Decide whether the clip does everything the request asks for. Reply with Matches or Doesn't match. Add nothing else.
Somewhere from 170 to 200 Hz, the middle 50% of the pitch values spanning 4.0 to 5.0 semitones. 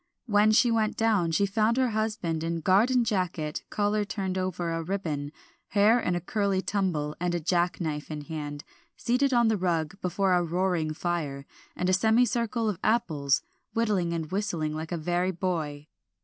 Matches